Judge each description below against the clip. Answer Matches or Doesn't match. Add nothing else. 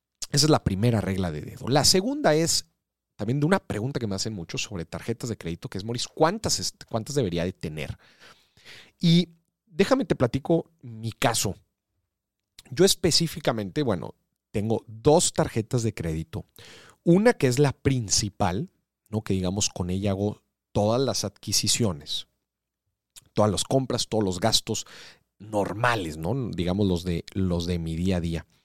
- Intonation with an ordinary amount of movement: Doesn't match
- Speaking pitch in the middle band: Doesn't match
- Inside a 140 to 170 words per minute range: Matches